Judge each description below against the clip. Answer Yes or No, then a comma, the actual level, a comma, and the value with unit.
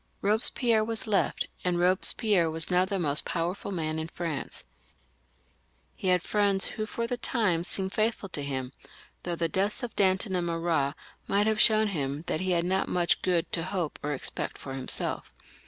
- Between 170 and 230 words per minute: Yes, average, 180 wpm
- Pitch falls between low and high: Yes, medium, 180 Hz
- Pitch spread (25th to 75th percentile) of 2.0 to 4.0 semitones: Yes, average, 3.7 semitones